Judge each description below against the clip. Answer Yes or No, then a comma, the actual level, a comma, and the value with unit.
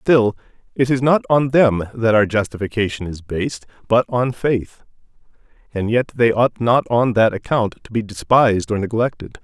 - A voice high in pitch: No, low, 115 Hz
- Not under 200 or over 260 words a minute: No, average, 170 wpm